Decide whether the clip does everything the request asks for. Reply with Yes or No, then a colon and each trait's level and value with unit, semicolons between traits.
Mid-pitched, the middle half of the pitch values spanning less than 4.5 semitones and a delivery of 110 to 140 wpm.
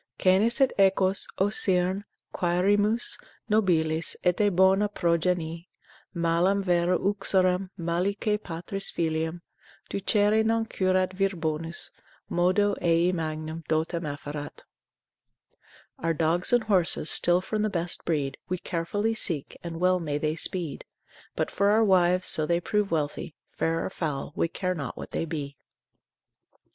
Yes: medium, 180 Hz; average, 3.1 semitones; slow, 135 wpm